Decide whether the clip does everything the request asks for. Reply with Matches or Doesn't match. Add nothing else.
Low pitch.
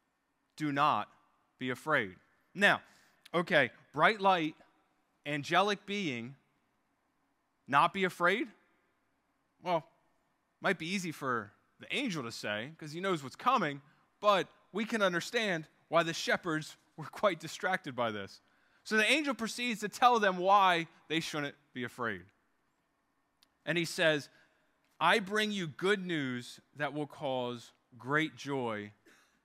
Doesn't match